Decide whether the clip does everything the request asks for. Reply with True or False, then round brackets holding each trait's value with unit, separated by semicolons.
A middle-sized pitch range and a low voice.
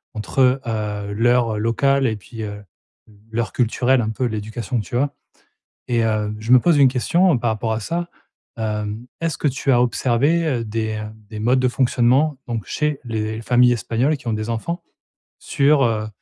True (3.5 semitones; 120 Hz)